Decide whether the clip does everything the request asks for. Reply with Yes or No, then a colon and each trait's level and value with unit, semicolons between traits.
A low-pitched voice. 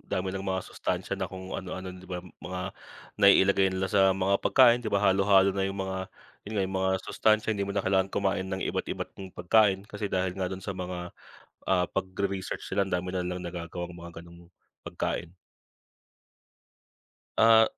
Yes: very low, 95 Hz